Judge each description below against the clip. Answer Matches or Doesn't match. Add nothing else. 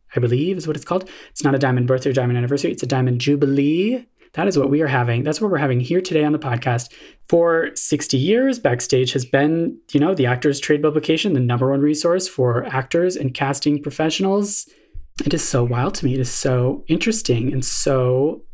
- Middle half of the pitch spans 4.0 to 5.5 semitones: Matches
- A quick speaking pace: Matches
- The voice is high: Doesn't match